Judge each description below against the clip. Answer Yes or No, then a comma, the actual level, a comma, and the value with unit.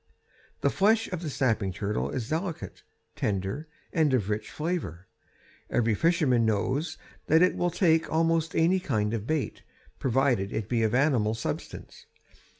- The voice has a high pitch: No, low, 135 Hz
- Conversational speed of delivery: Yes, average, 150 wpm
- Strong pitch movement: Yes, wide, 7.2 semitones